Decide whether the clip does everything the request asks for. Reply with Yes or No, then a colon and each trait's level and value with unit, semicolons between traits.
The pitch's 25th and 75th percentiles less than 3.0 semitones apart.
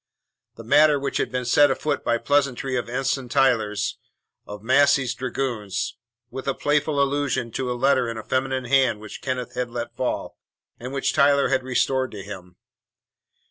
Yes: narrow, 2.5 semitones